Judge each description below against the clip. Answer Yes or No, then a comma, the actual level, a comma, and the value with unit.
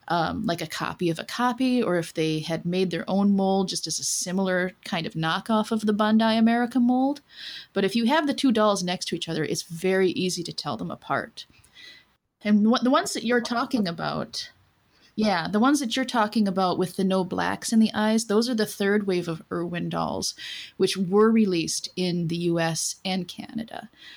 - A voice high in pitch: Yes, high, 200 Hz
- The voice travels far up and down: No, average, 4.5 semitones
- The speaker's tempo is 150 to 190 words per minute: No, fast, 205 wpm